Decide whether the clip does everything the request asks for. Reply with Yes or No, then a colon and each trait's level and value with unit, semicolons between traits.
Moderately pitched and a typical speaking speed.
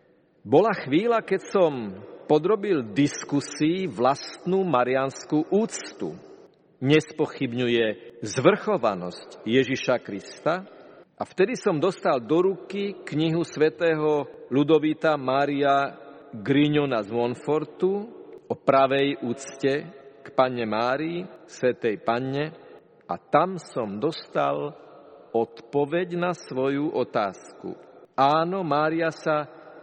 No: medium, 150 Hz; slow, 90 wpm